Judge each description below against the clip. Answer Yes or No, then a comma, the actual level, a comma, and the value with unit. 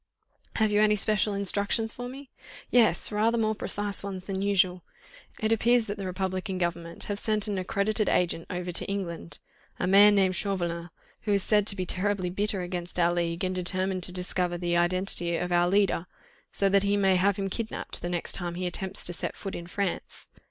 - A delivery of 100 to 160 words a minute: No, average, 200 wpm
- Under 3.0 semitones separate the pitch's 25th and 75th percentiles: Yes, narrow, 2.5 semitones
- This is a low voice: No, high, 190 Hz